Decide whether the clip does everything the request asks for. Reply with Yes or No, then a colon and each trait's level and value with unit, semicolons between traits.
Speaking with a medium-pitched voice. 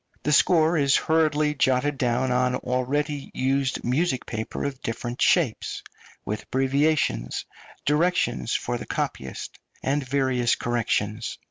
No: low, 130 Hz